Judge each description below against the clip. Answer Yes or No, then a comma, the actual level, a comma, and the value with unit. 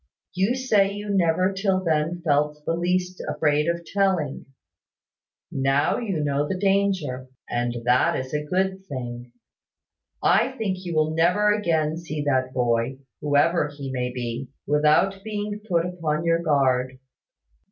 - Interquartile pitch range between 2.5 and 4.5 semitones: No, average, 5.2 semitones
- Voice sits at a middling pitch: Yes, medium, 160 Hz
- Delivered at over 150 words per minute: No, average, 140 wpm